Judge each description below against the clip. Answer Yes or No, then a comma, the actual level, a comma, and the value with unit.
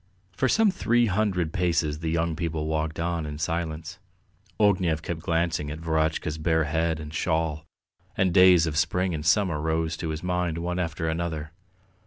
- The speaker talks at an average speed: Yes, average, 170 wpm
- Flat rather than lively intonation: Yes, narrow, 2.0 semitones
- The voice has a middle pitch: No, very low, 80 Hz